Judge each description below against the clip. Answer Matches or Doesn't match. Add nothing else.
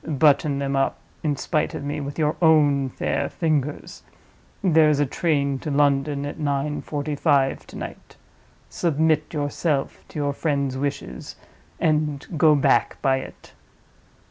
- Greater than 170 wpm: Doesn't match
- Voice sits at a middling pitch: Matches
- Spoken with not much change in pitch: Matches